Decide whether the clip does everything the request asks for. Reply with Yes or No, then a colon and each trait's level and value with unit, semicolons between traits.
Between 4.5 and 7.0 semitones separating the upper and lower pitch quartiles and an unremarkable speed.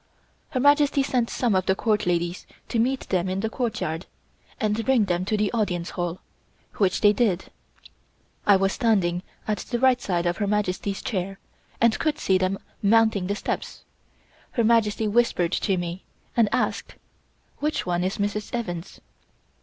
No: average, 4.0 semitones; average, 165 wpm